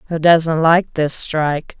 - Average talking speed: Yes, average, 165 wpm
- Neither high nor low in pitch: Yes, medium, 160 Hz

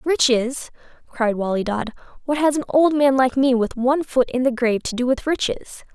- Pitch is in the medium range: No, very high, 260 Hz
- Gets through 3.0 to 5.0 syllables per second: No, 5.2 syllables/s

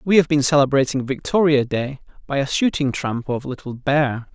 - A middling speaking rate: Yes, average, 180 wpm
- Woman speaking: No, male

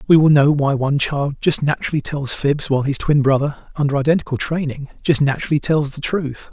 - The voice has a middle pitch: Yes, medium, 145 Hz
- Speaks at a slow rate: No, average, 200 wpm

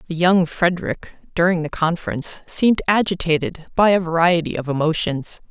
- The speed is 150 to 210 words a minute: No, average, 140 wpm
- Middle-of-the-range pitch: Yes, medium, 170 Hz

